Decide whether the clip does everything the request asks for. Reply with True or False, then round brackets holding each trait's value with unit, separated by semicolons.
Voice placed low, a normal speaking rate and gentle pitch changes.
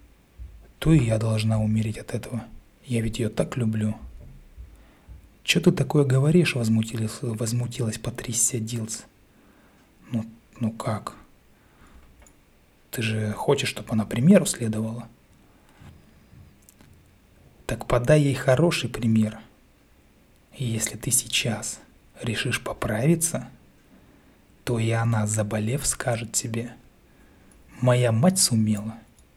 False (115 Hz; 100 wpm; 2.3 semitones)